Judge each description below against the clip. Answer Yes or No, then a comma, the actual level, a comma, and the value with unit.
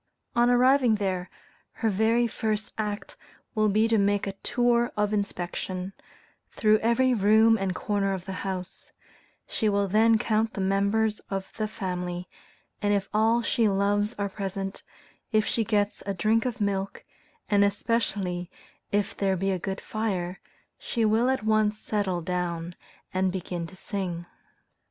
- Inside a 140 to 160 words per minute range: Yes, average, 155 wpm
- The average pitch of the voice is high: Yes, high, 205 Hz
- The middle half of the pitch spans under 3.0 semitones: Yes, narrow, 2.5 semitones